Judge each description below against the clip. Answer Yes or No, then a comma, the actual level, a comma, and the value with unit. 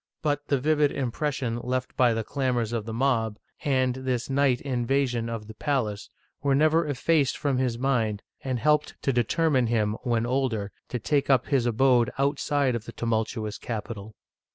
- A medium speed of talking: Yes, average, 170 wpm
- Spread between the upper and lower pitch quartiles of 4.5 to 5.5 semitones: No, average, 3.2 semitones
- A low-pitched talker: Yes, low, 125 Hz